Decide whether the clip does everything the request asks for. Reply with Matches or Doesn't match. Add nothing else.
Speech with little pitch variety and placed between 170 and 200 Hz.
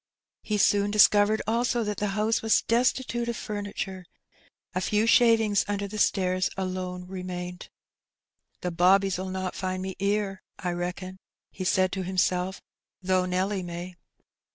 Matches